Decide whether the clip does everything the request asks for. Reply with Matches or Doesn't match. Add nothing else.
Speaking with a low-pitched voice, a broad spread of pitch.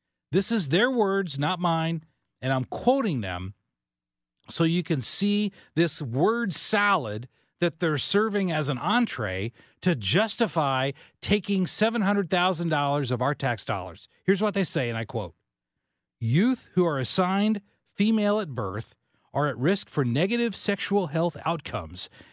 Doesn't match